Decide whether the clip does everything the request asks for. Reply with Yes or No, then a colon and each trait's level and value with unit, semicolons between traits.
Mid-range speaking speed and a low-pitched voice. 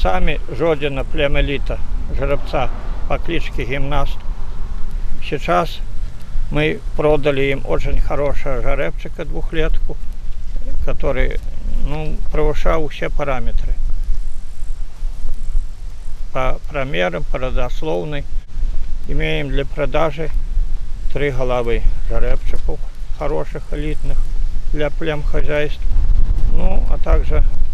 No: slow, 80 wpm; low, 130 Hz